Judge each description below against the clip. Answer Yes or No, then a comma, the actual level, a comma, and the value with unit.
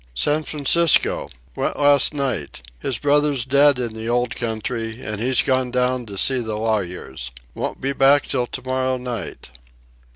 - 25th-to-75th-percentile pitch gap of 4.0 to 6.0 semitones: No, average, 3.5 semitones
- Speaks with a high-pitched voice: No, low, 125 Hz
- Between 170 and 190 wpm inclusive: No, average, 155 wpm